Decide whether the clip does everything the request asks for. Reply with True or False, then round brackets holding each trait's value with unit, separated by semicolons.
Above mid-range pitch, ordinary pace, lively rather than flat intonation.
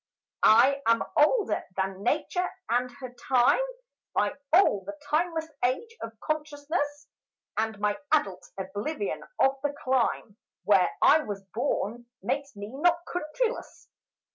False (275 Hz; 125 wpm; 5.8 semitones)